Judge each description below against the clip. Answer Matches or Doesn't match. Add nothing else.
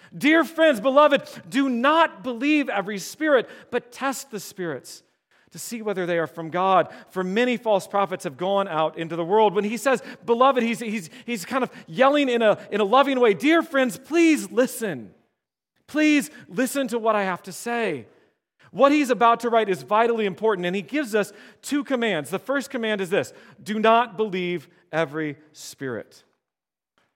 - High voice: Matches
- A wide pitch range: Matches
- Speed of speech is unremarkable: Matches